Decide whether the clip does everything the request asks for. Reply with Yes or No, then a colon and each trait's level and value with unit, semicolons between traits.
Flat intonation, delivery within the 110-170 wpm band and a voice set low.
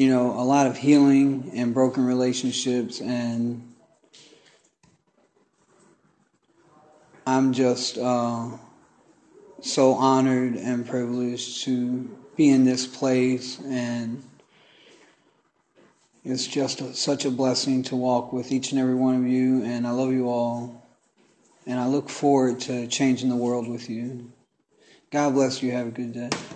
Yes: narrow, 1.4 semitones; slow, 135 wpm; low, 125 Hz